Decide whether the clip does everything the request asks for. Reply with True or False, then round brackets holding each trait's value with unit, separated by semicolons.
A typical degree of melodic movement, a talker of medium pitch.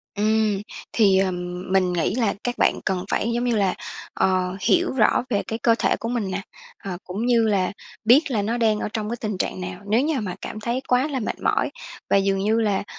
False (3.6 semitones; 215 Hz)